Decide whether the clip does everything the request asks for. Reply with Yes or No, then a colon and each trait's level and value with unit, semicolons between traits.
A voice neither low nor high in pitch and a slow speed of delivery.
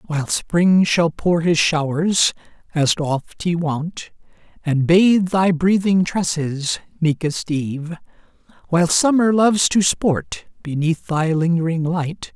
Yes: medium, 170 Hz; slow, 125 wpm